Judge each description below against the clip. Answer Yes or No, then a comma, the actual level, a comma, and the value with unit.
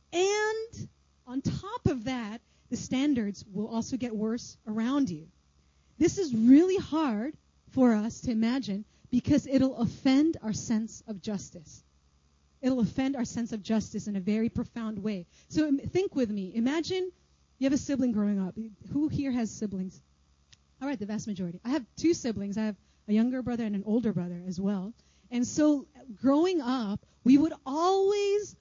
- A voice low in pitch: No, high, 235 Hz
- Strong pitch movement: No, average, 5.0 semitones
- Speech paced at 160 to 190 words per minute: Yes, average, 170 wpm